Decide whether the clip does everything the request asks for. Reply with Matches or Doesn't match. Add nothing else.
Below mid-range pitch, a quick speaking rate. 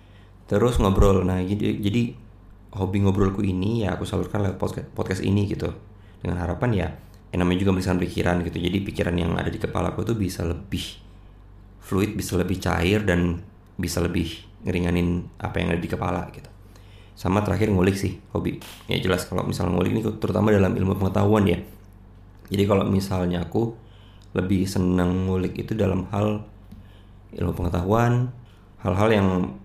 Matches